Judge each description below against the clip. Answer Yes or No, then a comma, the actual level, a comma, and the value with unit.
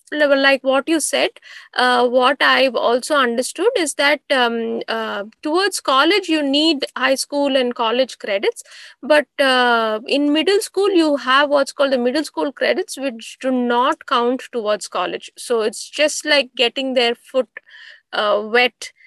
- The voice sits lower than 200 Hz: No, very high, 270 Hz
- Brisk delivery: Yes, fast, 160 wpm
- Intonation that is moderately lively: Yes, average, 3.5 semitones